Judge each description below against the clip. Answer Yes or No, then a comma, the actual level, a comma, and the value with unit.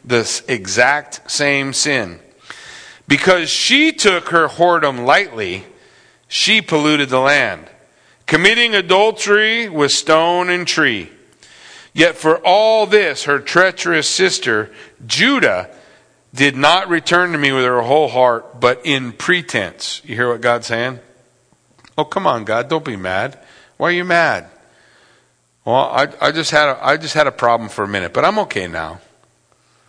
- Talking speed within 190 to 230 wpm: No, average, 150 wpm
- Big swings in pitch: Yes, wide, 5.9 semitones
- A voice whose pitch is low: No, medium, 155 Hz